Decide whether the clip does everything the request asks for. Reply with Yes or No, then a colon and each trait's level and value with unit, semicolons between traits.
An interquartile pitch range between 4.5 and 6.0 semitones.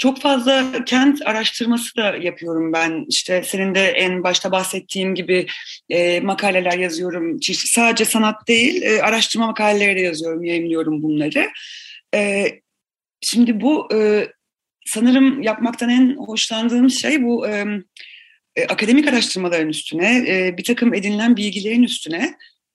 Yes: wide, 5.6 semitones